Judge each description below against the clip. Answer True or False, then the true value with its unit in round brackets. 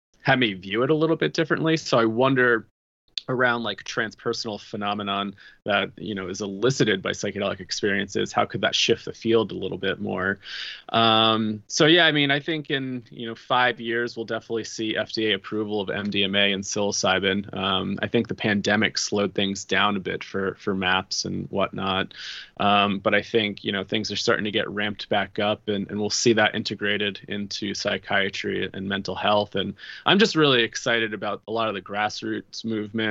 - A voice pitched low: True (110 Hz)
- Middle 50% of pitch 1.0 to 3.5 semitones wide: True (2.7 semitones)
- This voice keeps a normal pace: True (190 wpm)